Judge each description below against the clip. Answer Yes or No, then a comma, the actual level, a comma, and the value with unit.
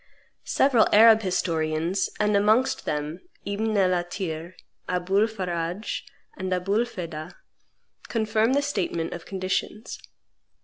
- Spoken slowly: Yes, slow, 105 wpm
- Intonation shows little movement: No, average, 3.8 semitones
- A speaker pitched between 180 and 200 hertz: Yes, high, 190 Hz